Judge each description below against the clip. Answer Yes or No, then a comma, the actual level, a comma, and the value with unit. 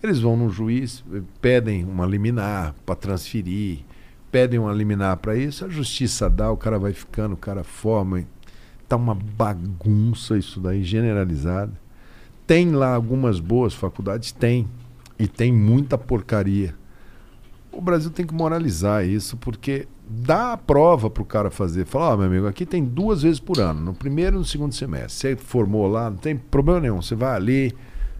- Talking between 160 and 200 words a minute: Yes, average, 170 wpm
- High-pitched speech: No, low, 115 Hz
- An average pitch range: Yes, average, 4.6 semitones